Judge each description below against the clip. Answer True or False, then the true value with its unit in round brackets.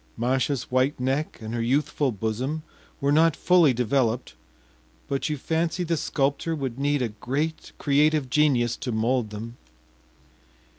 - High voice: False (135 Hz)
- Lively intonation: False (3.9 semitones)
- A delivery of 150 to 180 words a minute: False (140 wpm)